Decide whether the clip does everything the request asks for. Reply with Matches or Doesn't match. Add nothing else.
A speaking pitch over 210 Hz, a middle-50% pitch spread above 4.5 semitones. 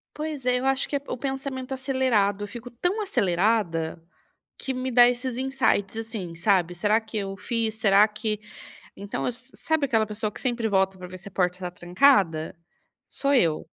Matches